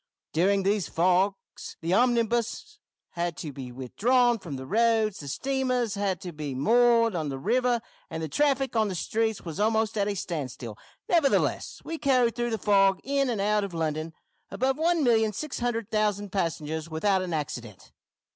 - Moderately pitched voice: No, high, 205 Hz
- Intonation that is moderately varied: No, wide, 6.4 semitones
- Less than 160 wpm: No, average, 170 wpm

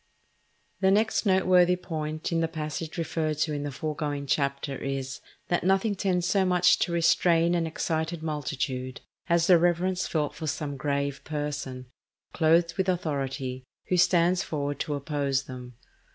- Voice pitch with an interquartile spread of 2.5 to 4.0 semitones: Yes, average, 3.7 semitones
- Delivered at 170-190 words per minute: No, average, 150 wpm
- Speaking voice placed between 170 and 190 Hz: No, medium, 160 Hz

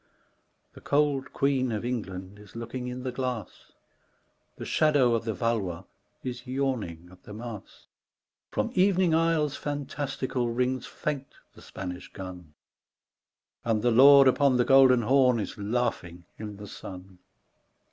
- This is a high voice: No, low, 125 Hz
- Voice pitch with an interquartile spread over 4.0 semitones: Yes, average, 4.7 semitones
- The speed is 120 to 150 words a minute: Yes, average, 140 wpm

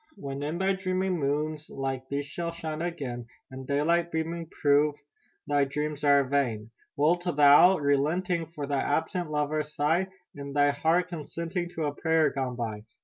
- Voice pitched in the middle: Yes, medium, 150 Hz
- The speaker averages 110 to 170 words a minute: Yes, average, 165 wpm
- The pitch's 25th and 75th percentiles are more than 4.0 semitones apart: No, average, 3.1 semitones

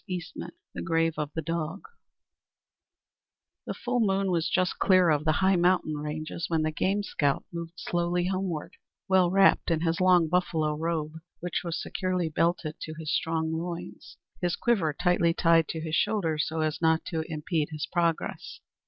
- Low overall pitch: No, medium, 165 Hz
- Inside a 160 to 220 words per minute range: Yes, average, 170 wpm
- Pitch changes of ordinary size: No, narrow, 2.3 semitones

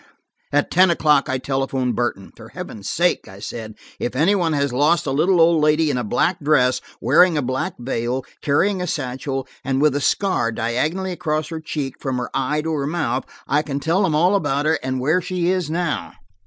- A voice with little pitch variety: No, average, 4.4 semitones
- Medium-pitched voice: Yes, medium, 145 Hz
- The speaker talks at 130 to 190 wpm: No, fast, 205 wpm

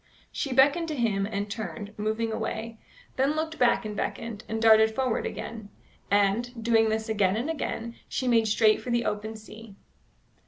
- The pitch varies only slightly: Yes, narrow, 1.9 semitones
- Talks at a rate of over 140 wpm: Yes, average, 170 wpm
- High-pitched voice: Yes, high, 225 Hz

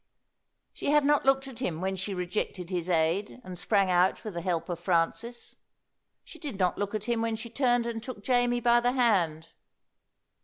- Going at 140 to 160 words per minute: No, average, 195 wpm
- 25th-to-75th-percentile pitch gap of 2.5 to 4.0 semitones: No, average, 5.1 semitones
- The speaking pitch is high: Yes, high, 210 Hz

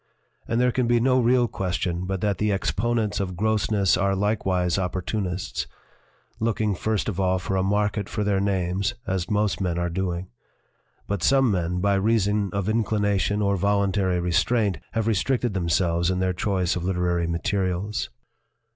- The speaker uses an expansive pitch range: No, average, 2.7 semitones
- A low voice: Yes, low, 100 Hz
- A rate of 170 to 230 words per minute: No, average, 160 wpm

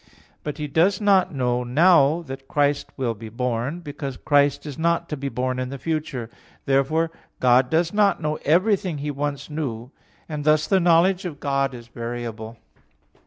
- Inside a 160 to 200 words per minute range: Yes, average, 170 wpm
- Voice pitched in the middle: Yes, medium, 145 Hz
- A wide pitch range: No, average, 4.3 semitones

